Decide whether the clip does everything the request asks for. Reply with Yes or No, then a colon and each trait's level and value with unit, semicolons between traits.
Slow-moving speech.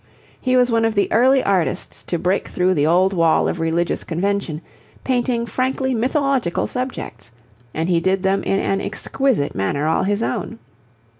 No: average, 165 wpm